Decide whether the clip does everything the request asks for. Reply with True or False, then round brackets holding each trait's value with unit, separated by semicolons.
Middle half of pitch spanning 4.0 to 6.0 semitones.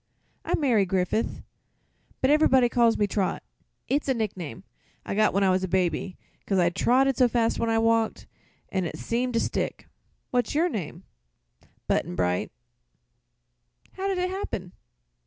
True (5.2 semitones)